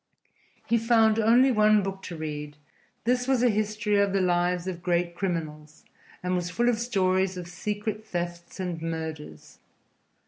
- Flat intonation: No, average, 3.9 semitones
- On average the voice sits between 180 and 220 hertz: Yes, medium, 185 Hz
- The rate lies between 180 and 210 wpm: No, average, 160 wpm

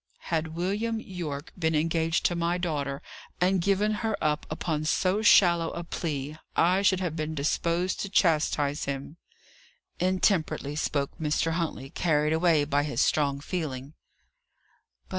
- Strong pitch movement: No, average, 3.2 semitones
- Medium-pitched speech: Yes, medium, 165 Hz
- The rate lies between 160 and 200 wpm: No, average, 140 wpm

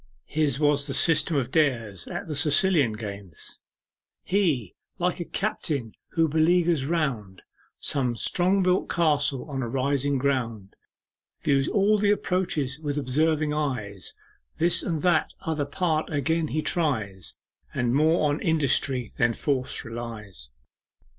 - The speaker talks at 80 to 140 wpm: Yes, slow, 135 wpm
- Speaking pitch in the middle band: Yes, medium, 145 Hz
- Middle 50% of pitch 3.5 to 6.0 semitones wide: Yes, average, 4.7 semitones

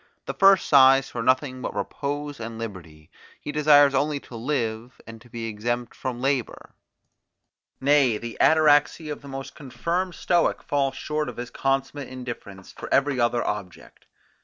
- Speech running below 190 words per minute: Yes, average, 160 wpm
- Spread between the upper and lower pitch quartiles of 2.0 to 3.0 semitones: No, average, 3.7 semitones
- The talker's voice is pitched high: No, low, 130 Hz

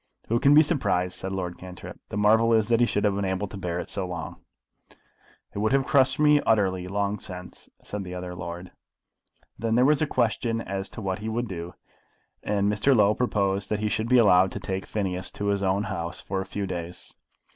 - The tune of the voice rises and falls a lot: No, average, 3.4 semitones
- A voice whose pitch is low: Yes, low, 100 Hz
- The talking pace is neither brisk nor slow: No, fast, 220 wpm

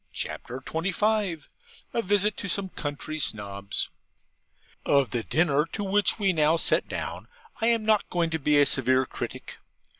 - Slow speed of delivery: No, average, 155 wpm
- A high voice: No, medium, 165 Hz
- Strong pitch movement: Yes, wide, 6.3 semitones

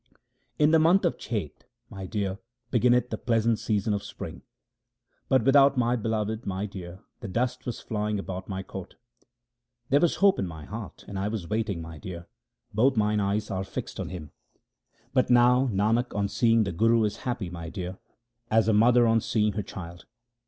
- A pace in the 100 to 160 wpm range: No, average, 190 wpm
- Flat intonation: No, average, 3.8 semitones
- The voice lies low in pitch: Yes, low, 105 Hz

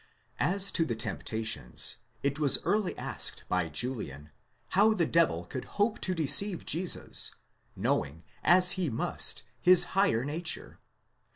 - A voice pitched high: No, medium, 165 Hz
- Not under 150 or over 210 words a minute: No, slow, 135 wpm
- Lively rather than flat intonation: Yes, wide, 8.5 semitones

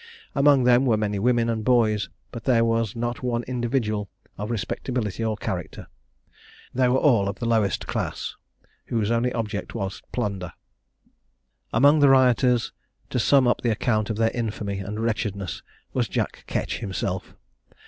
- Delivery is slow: No, average, 155 wpm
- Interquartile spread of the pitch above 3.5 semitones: No, average, 3.0 semitones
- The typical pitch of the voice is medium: No, low, 115 Hz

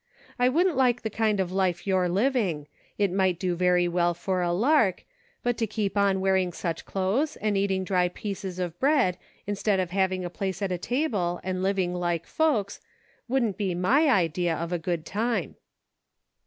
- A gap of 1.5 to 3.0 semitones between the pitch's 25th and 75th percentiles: No, average, 3.5 semitones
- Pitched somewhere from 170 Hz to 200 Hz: Yes, high, 190 Hz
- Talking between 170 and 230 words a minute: Yes, average, 185 wpm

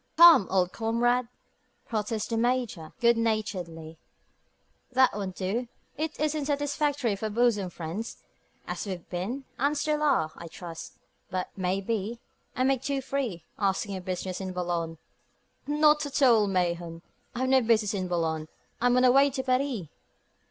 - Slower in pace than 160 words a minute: Yes, average, 150 wpm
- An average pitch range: No, wide, 6.1 semitones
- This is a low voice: No, high, 220 Hz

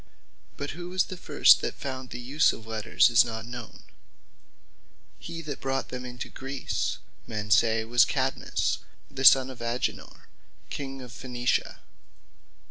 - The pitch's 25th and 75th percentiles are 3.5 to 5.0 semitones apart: No, narrow, 2.5 semitones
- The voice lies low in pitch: Yes, low, 125 Hz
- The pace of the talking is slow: No, average, 150 wpm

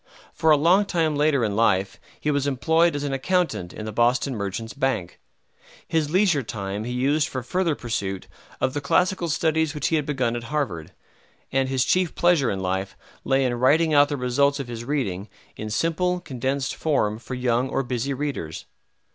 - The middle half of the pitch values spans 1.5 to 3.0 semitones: No, average, 4.9 semitones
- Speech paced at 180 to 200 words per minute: Yes, average, 190 wpm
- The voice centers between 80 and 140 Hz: Yes, low, 135 Hz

